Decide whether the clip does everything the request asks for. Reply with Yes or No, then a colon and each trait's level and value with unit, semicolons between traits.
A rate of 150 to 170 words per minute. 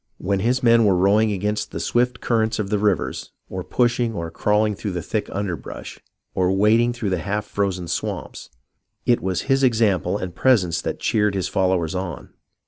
No: average, 180 wpm